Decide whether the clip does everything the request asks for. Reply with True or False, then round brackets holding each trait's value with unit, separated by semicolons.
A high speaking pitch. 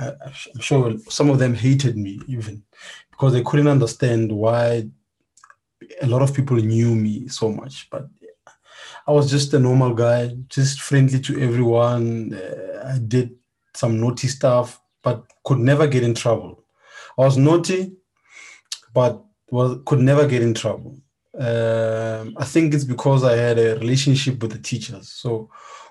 False (125 Hz)